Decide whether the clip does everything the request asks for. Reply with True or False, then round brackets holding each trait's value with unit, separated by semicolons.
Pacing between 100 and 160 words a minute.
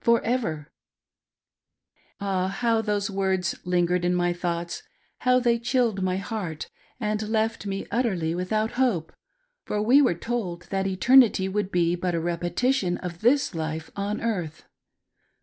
True (150 wpm)